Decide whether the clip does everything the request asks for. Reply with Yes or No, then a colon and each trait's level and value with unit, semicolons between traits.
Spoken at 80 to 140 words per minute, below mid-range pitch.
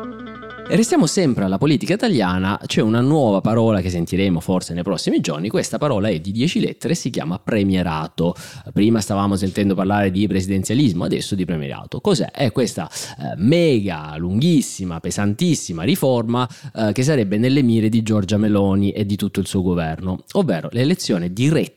No: average, 155 wpm; low, 105 Hz